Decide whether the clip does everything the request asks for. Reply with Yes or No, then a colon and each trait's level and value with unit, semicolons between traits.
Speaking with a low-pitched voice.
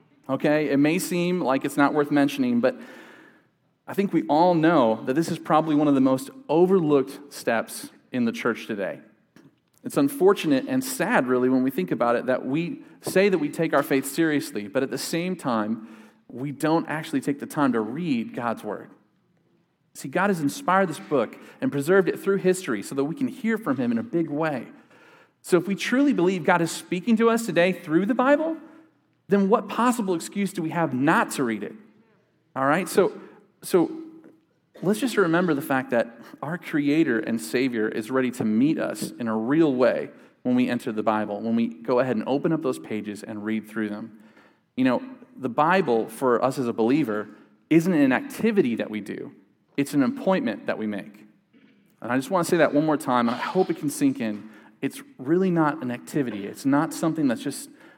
No: medium, 160 Hz